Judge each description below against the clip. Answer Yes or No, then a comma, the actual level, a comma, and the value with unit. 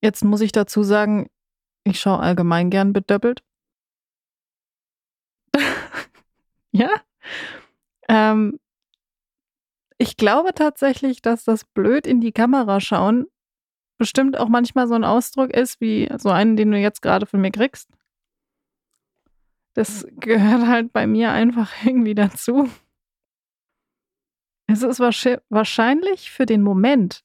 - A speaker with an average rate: No, slow, 115 wpm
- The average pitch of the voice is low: No, high, 230 Hz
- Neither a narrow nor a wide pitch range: Yes, average, 3.1 semitones